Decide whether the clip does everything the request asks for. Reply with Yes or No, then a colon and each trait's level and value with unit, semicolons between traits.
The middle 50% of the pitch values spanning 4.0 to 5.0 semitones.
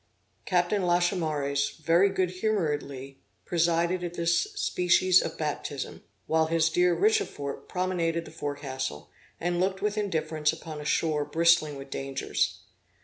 No: average, 3.3 semitones